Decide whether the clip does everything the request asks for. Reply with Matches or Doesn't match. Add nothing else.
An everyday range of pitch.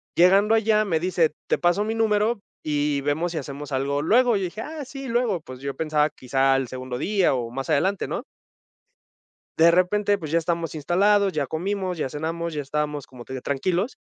Doesn't match